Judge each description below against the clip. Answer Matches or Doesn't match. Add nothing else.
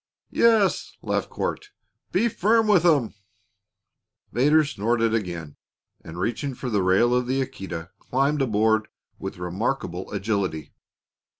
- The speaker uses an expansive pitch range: Matches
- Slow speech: Matches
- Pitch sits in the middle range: Doesn't match